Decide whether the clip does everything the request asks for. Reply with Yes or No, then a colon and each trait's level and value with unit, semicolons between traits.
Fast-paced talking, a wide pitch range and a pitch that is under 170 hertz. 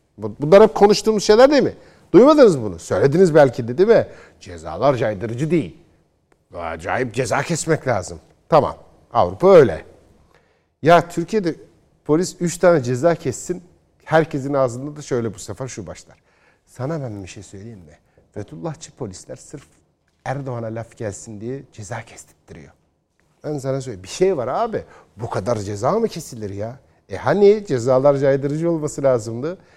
Yes: fast, 145 wpm; wide, 6.1 semitones; low, 135 Hz